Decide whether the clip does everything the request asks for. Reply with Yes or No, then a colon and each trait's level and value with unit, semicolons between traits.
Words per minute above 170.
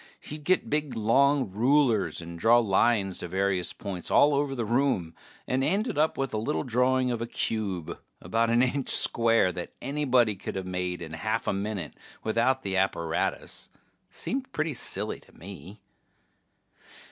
No: average, 165 wpm